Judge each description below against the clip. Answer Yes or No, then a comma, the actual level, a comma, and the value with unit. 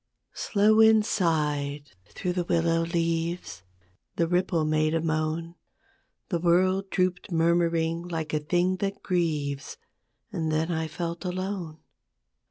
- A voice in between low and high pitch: Yes, medium, 170 Hz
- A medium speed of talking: No, slow, 125 wpm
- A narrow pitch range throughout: Yes, narrow, 2.2 semitones